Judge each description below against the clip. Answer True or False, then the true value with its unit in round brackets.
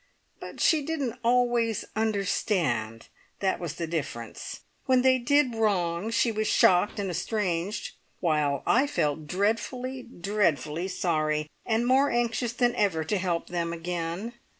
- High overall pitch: True (200 Hz)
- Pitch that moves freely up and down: True (6.1 semitones)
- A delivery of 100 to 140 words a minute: True (135 wpm)